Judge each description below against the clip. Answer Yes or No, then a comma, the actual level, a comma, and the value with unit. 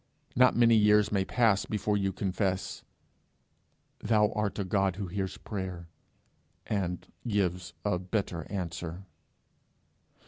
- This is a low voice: Yes, low, 100 Hz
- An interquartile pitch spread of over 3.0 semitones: No, narrow, 2.4 semitones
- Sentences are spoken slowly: Yes, slow, 115 wpm